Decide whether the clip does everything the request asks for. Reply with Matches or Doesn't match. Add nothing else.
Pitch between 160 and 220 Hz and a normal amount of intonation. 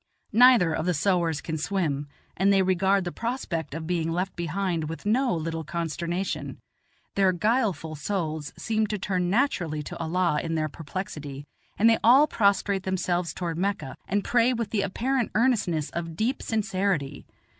Matches